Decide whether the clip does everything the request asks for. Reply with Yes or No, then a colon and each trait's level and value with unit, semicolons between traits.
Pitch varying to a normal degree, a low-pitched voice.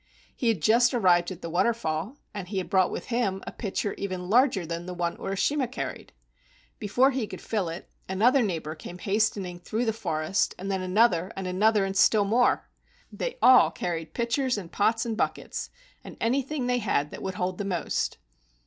No: average, 4.5 semitones; high, 195 Hz